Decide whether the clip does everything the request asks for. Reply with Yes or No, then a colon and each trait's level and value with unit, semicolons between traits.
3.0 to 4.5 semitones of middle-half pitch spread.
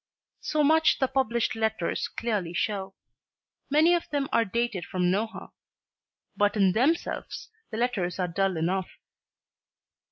No: wide, 5.5 semitones